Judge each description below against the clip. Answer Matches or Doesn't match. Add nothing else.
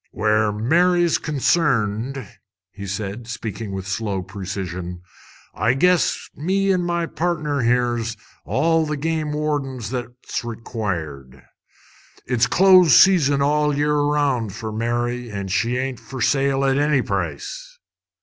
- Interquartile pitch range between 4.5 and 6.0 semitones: Matches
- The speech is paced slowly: Matches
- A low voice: Matches